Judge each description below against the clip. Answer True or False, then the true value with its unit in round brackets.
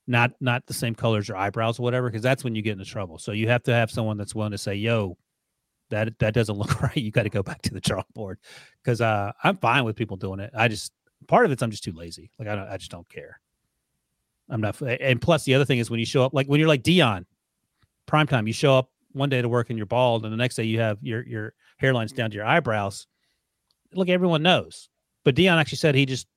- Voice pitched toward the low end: True (115 Hz)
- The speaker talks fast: True (260 wpm)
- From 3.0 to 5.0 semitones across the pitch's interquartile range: True (3.7 semitones)